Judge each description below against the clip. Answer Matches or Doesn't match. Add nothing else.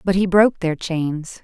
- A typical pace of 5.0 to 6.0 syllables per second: Doesn't match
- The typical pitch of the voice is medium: Matches